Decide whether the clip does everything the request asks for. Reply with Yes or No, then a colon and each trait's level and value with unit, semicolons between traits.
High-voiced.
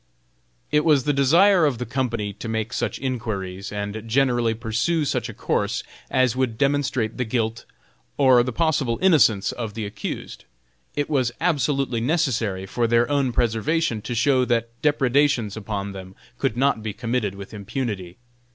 No: low, 120 Hz